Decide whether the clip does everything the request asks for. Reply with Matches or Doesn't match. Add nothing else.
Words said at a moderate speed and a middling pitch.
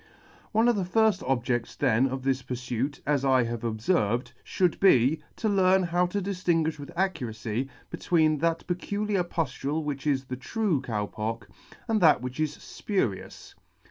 Matches